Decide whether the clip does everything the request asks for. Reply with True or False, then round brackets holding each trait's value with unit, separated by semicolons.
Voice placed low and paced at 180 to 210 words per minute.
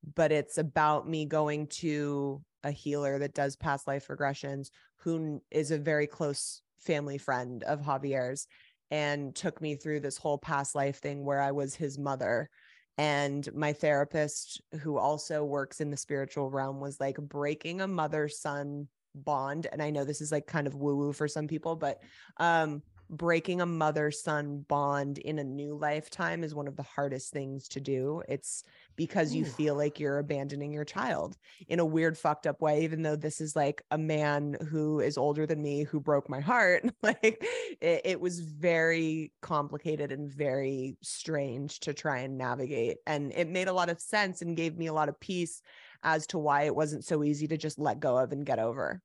False (150 Hz; 195 wpm)